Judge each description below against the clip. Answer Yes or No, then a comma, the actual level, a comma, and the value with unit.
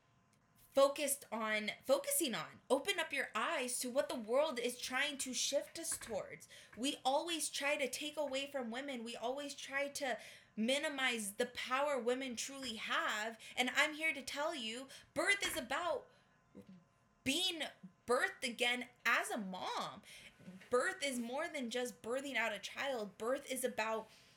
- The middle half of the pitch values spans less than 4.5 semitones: Yes, average, 2.9 semitones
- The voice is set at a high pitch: Yes, very high, 260 Hz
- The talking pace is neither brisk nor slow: Yes, average, 155 wpm